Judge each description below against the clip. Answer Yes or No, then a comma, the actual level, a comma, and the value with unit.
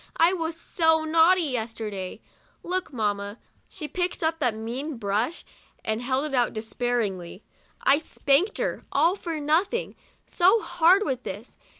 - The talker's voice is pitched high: Yes, very high, 285 Hz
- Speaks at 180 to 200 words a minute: No, average, 160 wpm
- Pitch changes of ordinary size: No, wide, 6.8 semitones